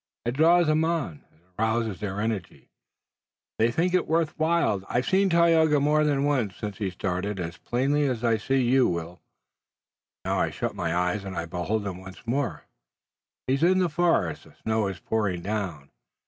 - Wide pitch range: Yes, wide, 8.1 semitones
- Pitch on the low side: Yes, low, 110 Hz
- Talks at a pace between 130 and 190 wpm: Yes, average, 180 wpm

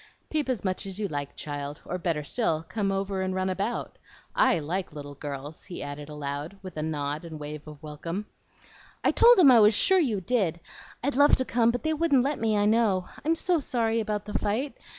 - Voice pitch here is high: Yes, high, 195 Hz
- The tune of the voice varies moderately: No, wide, 7.6 semitones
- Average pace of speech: No, fast, 220 wpm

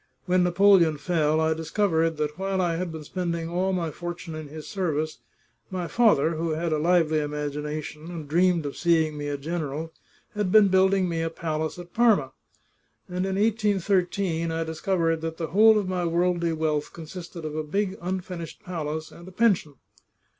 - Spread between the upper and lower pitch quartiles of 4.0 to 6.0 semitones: No, average, 2.9 semitones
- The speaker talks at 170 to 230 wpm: Yes, average, 180 wpm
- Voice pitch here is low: No, medium, 170 Hz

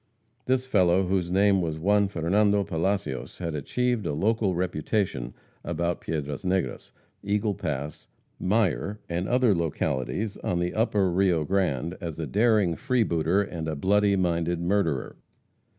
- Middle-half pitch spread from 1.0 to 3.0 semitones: No, average, 3.8 semitones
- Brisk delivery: No, slow, 135 wpm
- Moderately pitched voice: No, very low, 90 Hz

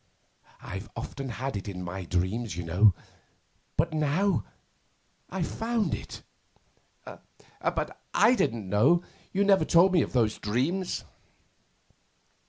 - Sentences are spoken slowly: Yes, slow, 120 wpm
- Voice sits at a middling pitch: No, low, 125 Hz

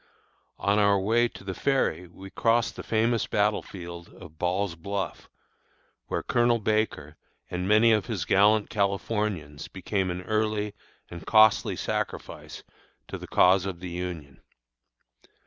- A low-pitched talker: Yes, low, 100 Hz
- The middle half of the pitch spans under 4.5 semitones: Yes, average, 3.4 semitones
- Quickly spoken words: No, average, 140 wpm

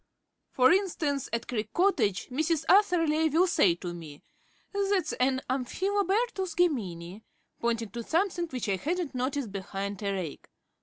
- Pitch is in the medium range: No, very high, 270 Hz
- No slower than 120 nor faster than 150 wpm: Yes, average, 140 wpm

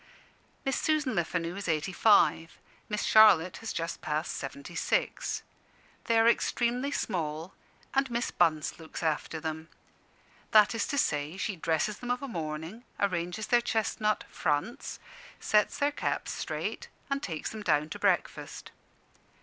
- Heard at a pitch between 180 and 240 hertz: Yes, medium, 185 Hz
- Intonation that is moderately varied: No, wide, 6.2 semitones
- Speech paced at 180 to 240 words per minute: No, average, 145 wpm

